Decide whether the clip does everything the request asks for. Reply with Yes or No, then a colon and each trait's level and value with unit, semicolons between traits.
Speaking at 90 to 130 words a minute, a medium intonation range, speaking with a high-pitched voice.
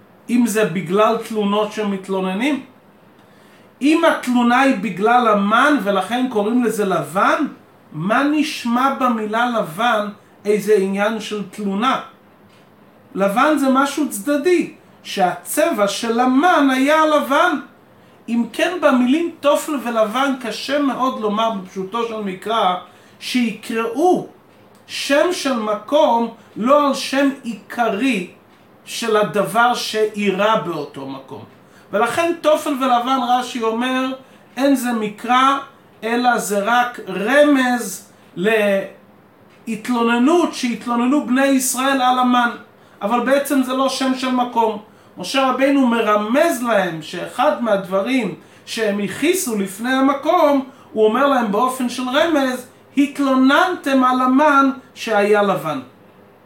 Yes: average, 105 wpm; average, 4.5 semitones; high, 245 Hz